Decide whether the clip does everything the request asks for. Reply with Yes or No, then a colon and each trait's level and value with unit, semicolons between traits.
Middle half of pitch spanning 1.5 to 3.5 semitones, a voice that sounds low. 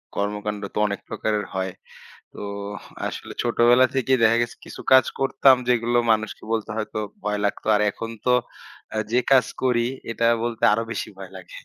Yes: average, 2.7 semitones; low, 115 Hz